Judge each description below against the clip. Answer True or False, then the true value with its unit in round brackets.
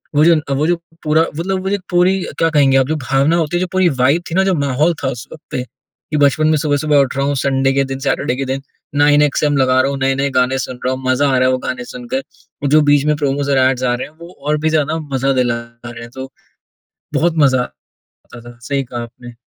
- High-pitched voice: False (140 Hz)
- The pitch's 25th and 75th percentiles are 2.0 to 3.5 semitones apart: True (2.9 semitones)